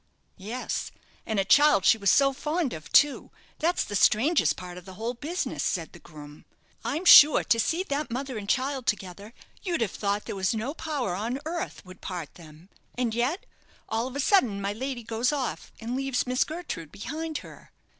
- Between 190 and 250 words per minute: Yes, average, 195 wpm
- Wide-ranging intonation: Yes, wide, 6.4 semitones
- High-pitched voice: Yes, high, 235 Hz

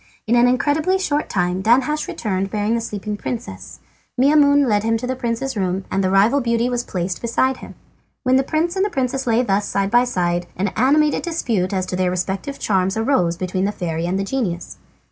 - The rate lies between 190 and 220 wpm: Yes, fast, 205 wpm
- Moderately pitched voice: No, high, 225 Hz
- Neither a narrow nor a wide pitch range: No, wide, 5.7 semitones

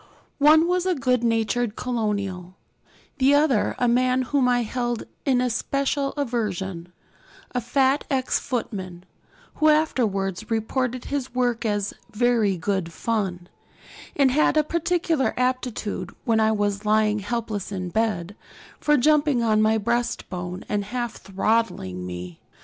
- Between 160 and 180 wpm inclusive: No, slow, 135 wpm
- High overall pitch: Yes, high, 230 Hz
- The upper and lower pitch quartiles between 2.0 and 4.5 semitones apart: Yes, average, 4.2 semitones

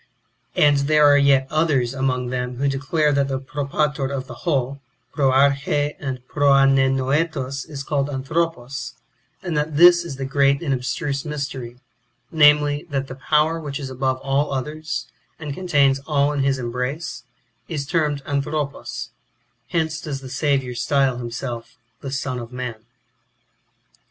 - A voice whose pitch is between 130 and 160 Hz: Yes, medium, 140 Hz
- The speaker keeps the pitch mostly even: Yes, narrow, 2.0 semitones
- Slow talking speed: No, average, 145 wpm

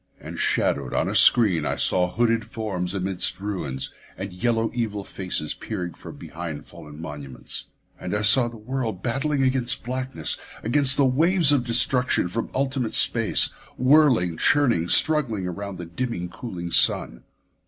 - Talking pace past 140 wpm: Yes, average, 150 wpm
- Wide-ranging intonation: Yes, wide, 6.4 semitones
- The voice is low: Yes, low, 110 Hz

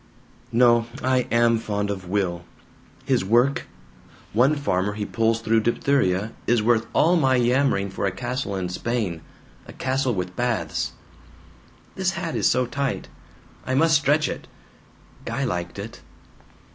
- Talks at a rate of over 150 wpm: No, average, 145 wpm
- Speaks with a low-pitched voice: Yes, low, 120 Hz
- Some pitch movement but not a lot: Yes, average, 4.5 semitones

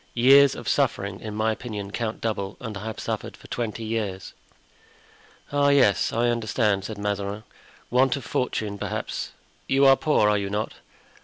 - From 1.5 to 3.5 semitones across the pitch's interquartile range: Yes, average, 3.2 semitones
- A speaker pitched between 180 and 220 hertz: No, low, 110 Hz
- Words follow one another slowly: No, average, 165 wpm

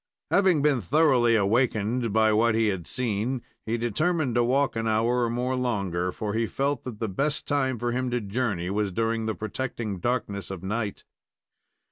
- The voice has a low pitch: Yes, low, 115 Hz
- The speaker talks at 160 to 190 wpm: Yes, average, 180 wpm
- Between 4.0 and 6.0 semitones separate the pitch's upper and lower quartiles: No, average, 3.2 semitones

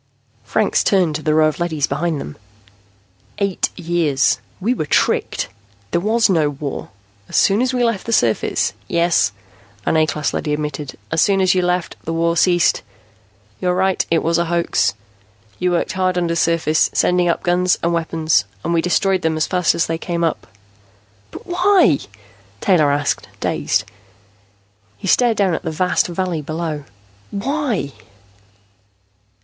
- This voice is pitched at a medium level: Yes, medium, 170 Hz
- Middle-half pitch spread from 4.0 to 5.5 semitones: No, average, 2.9 semitones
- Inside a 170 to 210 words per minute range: No, average, 160 wpm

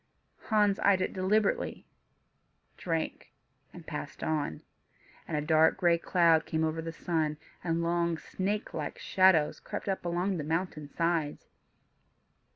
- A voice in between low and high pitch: Yes, medium, 170 Hz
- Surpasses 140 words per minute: No, slow, 135 wpm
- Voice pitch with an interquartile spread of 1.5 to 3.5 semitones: Yes, average, 2.8 semitones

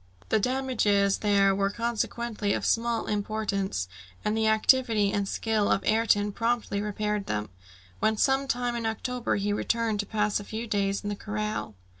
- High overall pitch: Yes, high, 215 Hz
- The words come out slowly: No, average, 165 wpm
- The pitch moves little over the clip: Yes, narrow, 2.3 semitones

